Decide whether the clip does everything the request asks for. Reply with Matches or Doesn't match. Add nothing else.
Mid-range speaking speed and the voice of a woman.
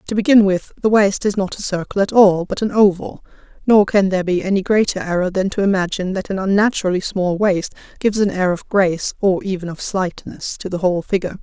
Doesn't match